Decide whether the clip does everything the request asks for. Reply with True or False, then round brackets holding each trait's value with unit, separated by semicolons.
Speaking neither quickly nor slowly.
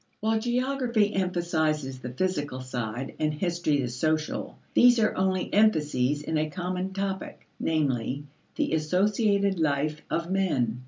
False (130 wpm)